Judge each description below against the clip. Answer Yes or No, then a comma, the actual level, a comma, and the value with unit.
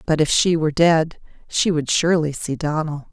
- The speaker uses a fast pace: No, average, 190 wpm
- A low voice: No, medium, 160 Hz